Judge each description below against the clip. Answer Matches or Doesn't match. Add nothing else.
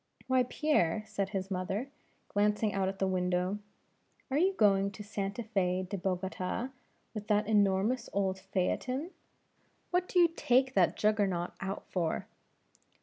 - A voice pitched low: Doesn't match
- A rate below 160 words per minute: Matches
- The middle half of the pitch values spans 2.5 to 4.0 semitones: Matches